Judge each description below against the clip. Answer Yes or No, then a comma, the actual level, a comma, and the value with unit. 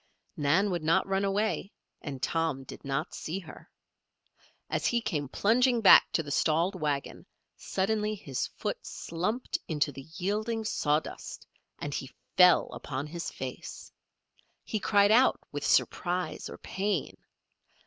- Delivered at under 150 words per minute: Yes, average, 140 wpm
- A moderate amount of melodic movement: No, wide, 5.7 semitones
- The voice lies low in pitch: No, medium, 180 Hz